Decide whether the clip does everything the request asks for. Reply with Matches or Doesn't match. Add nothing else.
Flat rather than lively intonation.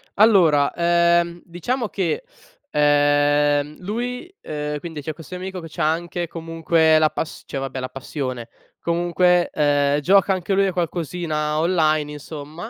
Doesn't match